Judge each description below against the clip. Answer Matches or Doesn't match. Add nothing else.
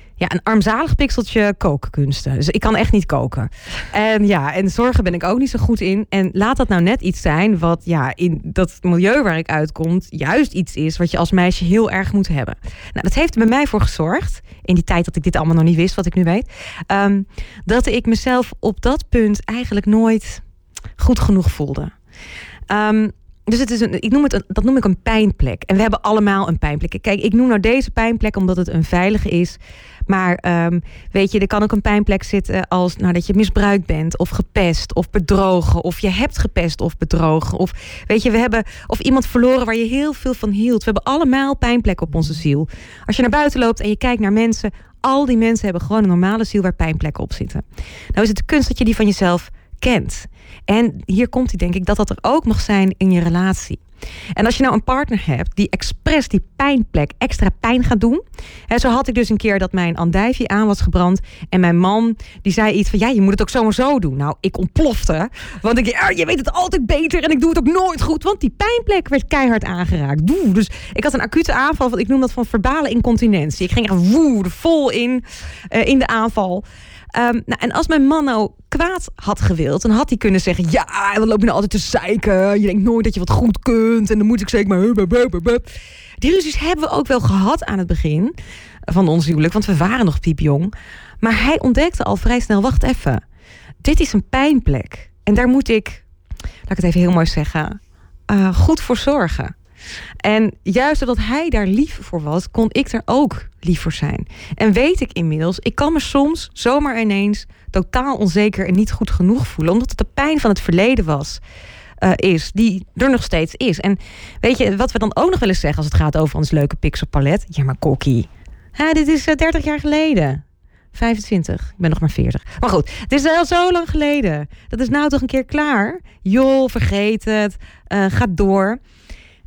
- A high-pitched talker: Matches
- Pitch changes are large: Matches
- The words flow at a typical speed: Doesn't match